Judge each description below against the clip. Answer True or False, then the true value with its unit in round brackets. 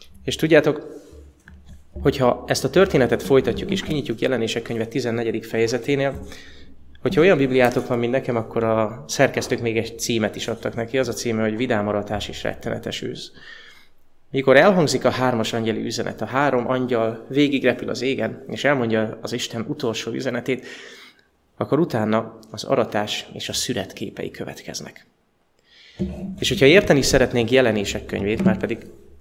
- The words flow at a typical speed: True (145 wpm)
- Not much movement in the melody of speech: False (3.2 semitones)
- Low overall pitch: True (115 Hz)